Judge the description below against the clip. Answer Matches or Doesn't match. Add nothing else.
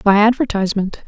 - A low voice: Doesn't match